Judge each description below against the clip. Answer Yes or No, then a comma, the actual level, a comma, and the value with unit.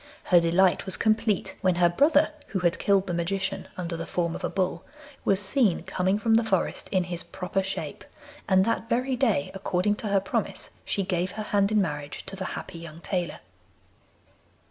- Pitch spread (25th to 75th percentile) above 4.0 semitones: No, average, 2.8 semitones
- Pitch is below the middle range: No, high, 190 Hz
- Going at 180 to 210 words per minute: Yes, average, 190 wpm